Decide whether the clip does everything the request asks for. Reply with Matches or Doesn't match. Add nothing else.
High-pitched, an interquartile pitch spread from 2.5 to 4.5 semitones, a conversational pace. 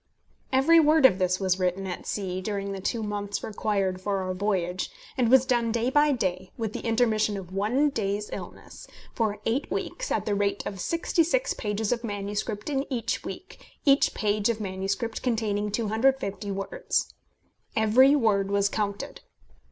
Matches